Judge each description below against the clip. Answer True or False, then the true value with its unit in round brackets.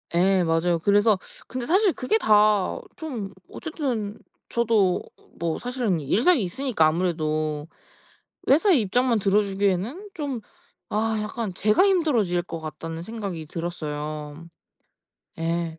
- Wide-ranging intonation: True (6.5 semitones)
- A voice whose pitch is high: True (200 Hz)